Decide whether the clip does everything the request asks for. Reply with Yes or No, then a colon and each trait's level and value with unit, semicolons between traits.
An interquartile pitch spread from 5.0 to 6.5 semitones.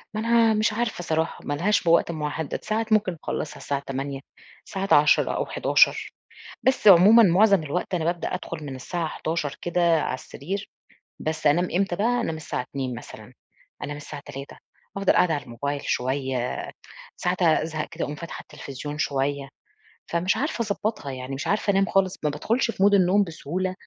Yes: wide, 5.4 semitones